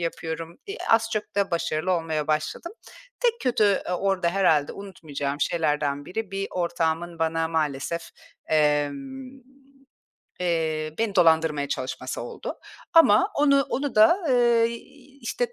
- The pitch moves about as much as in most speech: No, wide, 6.4 semitones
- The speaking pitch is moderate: Yes, medium, 170 Hz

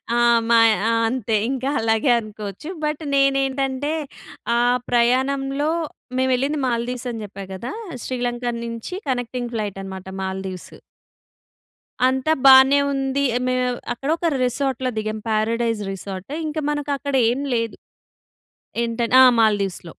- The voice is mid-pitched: No, high, 245 Hz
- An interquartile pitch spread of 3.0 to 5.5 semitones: Yes, average, 3.6 semitones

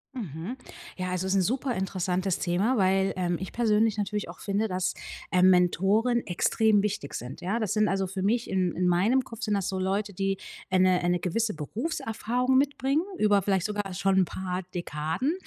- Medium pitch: No, high, 195 Hz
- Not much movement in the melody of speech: No, average, 3.2 semitones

